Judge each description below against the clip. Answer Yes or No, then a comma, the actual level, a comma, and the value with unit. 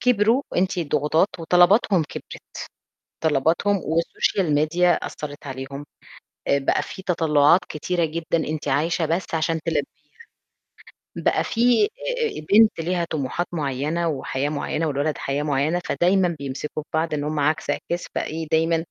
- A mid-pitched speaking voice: Yes, medium, 160 Hz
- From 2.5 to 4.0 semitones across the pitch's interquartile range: Yes, average, 3.3 semitones